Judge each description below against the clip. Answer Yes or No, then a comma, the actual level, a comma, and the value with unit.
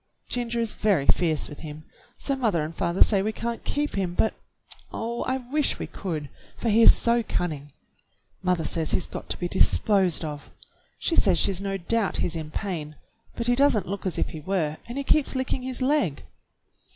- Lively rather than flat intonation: Yes, wide, 6.3 semitones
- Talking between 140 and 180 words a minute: No, average, 200 wpm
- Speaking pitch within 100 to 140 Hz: No, high, 195 Hz